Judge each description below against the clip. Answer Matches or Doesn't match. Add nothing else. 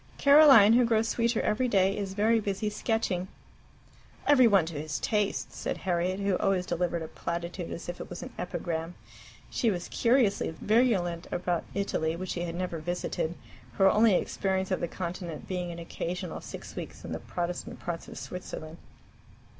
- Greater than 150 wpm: Matches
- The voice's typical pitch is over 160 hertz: Matches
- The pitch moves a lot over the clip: Doesn't match